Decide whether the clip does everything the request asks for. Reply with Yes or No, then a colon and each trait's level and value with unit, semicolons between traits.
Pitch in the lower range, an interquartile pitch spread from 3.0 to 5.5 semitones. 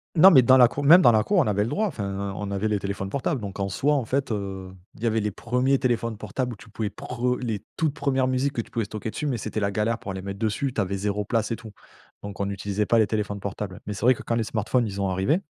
Yes: low, 110 Hz; average, 4.1 semitones